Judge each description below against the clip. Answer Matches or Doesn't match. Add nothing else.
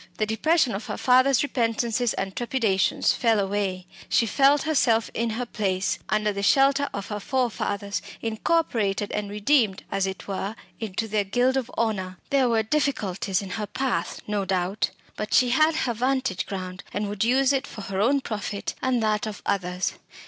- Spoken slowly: Doesn't match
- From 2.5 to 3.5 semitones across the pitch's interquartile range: Doesn't match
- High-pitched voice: Matches